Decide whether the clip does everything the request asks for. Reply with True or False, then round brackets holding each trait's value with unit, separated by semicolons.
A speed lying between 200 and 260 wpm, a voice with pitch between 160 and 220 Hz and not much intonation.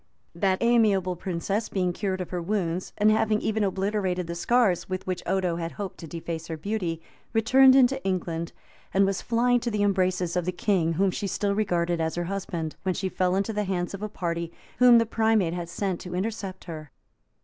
False (205 wpm; 190 Hz; 3.3 semitones)